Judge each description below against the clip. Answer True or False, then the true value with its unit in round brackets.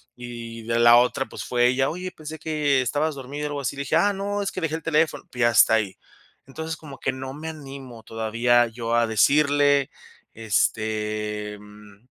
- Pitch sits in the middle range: False (130 Hz)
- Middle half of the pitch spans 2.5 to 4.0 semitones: False (4.7 semitones)